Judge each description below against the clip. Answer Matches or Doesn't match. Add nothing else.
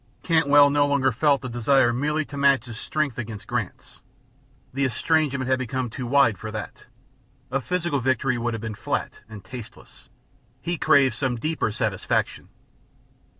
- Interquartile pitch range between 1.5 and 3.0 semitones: Doesn't match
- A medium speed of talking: Matches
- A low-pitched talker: Matches